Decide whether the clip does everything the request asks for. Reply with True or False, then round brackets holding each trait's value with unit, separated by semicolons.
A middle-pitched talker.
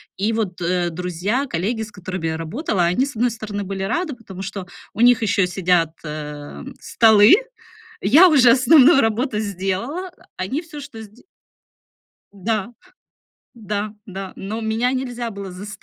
False (210 Hz)